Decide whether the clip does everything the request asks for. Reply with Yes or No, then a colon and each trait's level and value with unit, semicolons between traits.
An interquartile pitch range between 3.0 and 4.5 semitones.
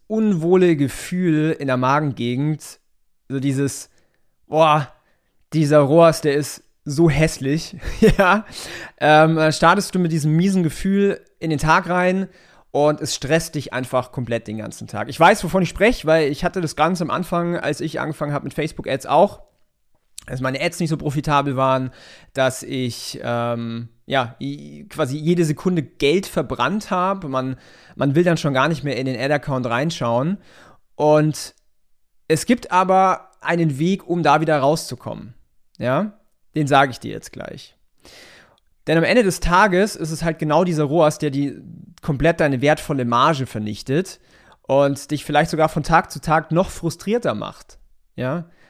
Yes: average, 3.8 semitones